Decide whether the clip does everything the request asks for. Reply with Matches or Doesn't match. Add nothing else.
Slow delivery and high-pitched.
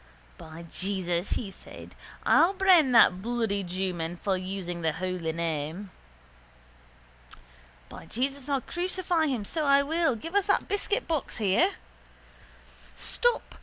Matches